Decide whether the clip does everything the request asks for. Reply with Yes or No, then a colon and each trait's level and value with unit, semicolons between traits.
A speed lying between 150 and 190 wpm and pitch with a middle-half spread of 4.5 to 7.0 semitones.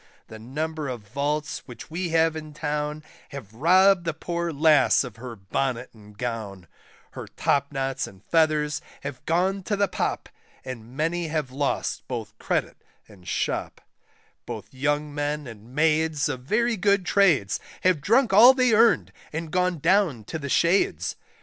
Yes: average, 155 wpm; average, 5.0 semitones